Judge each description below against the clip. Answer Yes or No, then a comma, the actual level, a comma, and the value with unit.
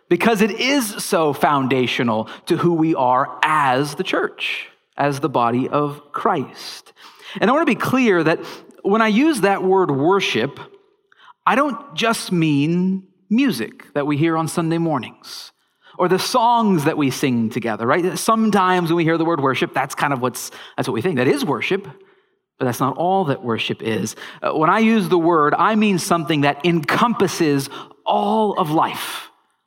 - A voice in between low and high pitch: Yes, medium, 175 Hz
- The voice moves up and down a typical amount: No, wide, 7.1 semitones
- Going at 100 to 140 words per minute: No, average, 175 wpm